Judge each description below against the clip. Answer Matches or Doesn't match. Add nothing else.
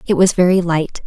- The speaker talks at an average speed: Doesn't match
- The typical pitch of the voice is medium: Matches